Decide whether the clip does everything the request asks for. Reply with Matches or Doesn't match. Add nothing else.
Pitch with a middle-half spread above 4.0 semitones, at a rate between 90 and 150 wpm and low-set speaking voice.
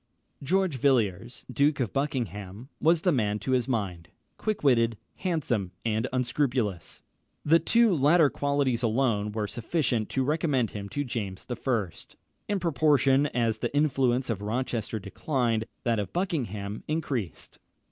Matches